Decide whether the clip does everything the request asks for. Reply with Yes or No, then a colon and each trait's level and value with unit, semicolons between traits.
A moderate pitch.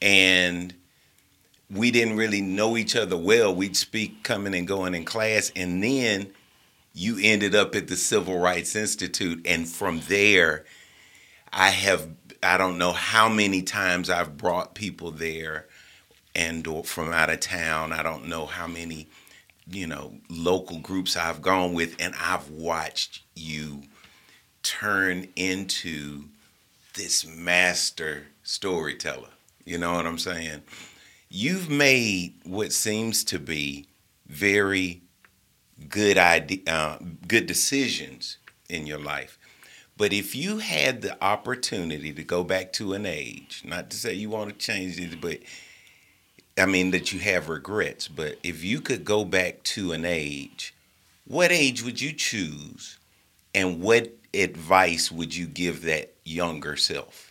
No: very low, 90 Hz